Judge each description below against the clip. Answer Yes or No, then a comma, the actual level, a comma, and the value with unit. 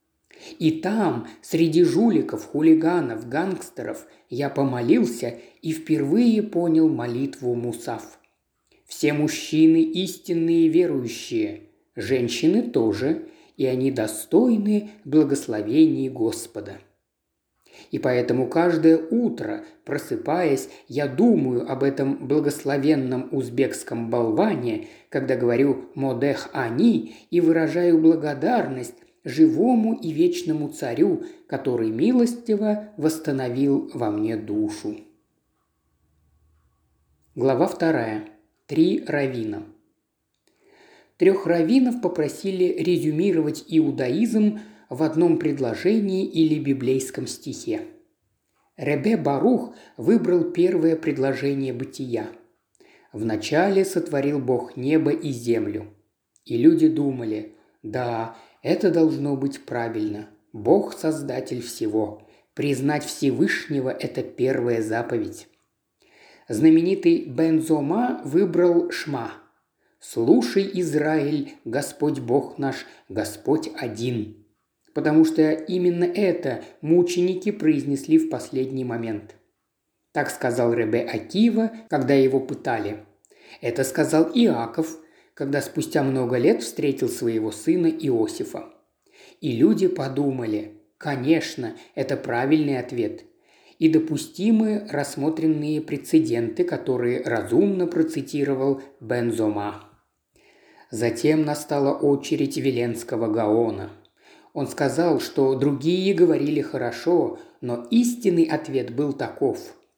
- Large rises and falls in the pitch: Yes, wide, 6.7 semitones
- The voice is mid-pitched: Yes, medium, 155 Hz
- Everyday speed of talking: No, slow, 90 wpm